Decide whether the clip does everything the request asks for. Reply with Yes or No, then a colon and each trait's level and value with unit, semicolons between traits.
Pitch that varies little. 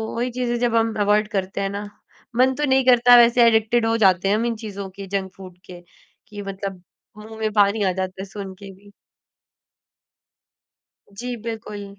No: average, 3.0 semitones